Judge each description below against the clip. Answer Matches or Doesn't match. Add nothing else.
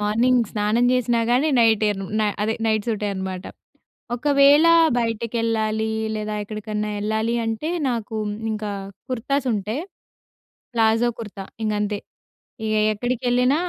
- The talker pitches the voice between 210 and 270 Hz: Matches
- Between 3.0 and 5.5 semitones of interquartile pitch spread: Doesn't match